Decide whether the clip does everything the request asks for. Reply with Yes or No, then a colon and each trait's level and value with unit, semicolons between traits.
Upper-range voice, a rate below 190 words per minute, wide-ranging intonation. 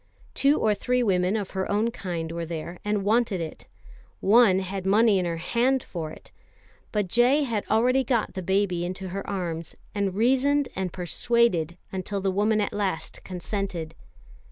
No: high, 195 Hz; average, 170 wpm; average, 4.1 semitones